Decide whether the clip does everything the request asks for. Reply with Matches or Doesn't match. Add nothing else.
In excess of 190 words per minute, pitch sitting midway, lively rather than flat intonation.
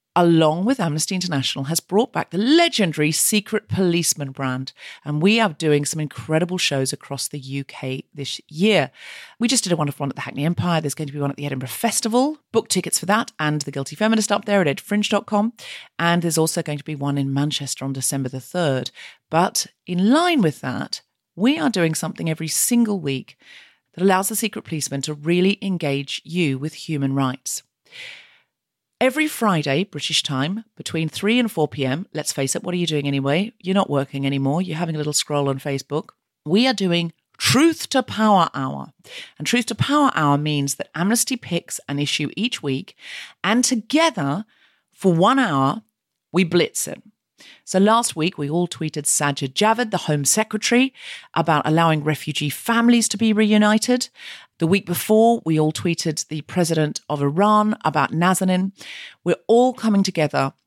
Doesn't match